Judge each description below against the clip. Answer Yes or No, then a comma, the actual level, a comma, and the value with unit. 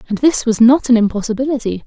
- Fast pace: No, average, 195 wpm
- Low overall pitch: No, high, 240 Hz